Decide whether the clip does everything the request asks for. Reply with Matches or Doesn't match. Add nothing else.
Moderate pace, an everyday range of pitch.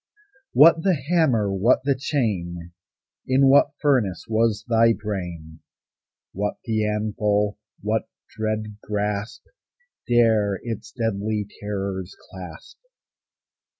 Doesn't match